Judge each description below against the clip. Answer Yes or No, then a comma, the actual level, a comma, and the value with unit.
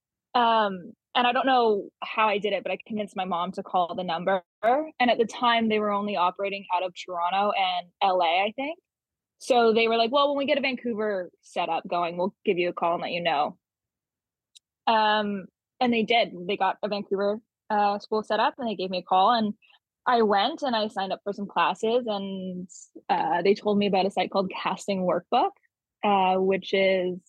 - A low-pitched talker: No, high, 205 Hz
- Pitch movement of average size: Yes, average, 3.7 semitones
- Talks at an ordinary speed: No, fast, 215 wpm